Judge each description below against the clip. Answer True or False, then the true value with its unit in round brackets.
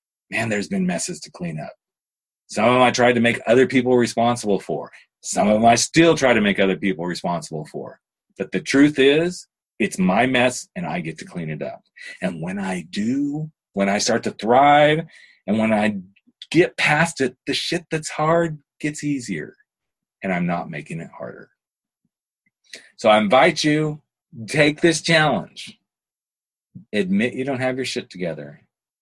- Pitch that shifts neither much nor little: False (6.6 semitones)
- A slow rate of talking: False (175 wpm)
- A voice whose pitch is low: False (150 Hz)